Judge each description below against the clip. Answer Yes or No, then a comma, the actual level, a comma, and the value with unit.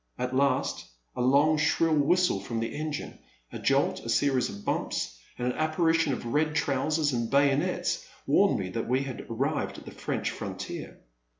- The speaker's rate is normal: Yes, average, 175 wpm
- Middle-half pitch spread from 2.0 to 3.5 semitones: No, average, 3.9 semitones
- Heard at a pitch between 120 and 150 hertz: Yes, medium, 140 Hz